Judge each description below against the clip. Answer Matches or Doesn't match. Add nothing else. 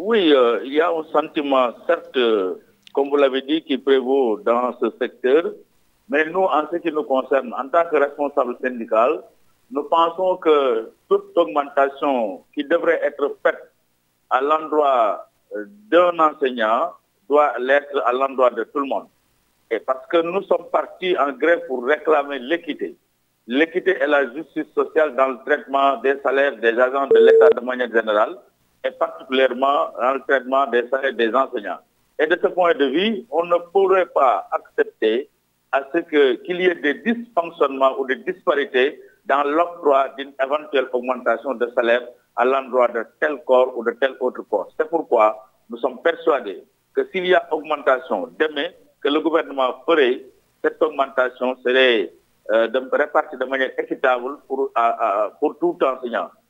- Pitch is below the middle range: Doesn't match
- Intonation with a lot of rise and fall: Matches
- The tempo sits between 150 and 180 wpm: Matches